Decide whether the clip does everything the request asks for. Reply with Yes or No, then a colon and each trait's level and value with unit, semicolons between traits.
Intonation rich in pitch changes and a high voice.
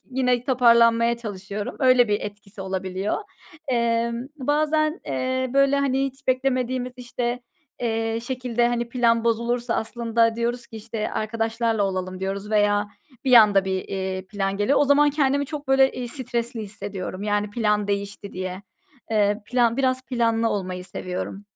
No: average, 3.6 semitones; high, 230 Hz